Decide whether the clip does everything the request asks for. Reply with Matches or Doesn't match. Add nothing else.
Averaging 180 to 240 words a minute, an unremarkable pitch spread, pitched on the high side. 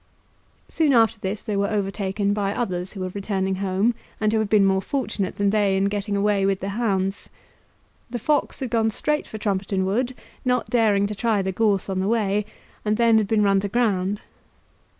Doesn't match